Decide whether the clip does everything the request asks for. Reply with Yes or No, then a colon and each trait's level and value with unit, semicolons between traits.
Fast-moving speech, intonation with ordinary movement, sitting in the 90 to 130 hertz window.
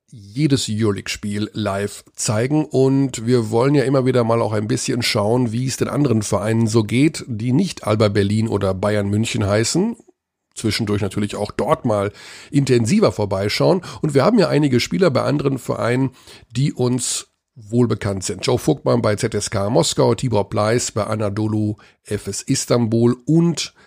No: average, 160 wpm; average, 3.7 semitones; low, 115 Hz